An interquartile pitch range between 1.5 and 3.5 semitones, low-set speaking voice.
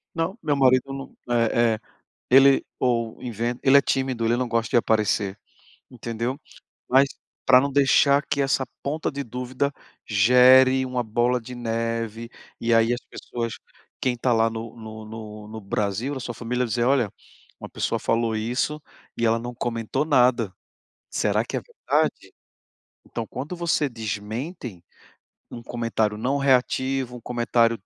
Yes: narrow, 2.5 semitones; low, 120 Hz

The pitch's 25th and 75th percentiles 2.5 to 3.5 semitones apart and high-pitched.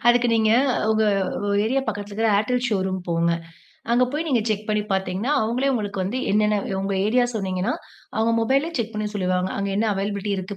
Yes: average, 3.1 semitones; high, 210 Hz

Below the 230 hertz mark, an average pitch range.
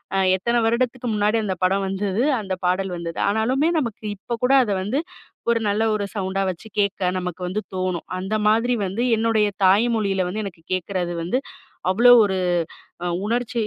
Yes: high, 205 Hz; average, 3.5 semitones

